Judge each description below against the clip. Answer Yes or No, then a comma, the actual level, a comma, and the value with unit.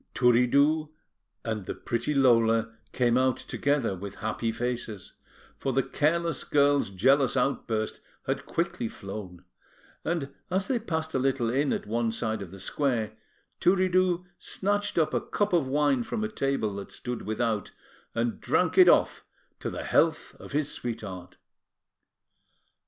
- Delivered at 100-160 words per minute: Yes, average, 145 wpm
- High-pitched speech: No, low, 125 Hz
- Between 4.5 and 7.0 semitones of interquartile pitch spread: Yes, average, 5.0 semitones